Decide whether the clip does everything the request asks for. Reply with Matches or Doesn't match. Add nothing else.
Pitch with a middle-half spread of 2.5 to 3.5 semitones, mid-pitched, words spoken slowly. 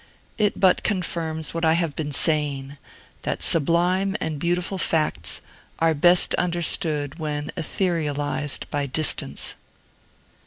Matches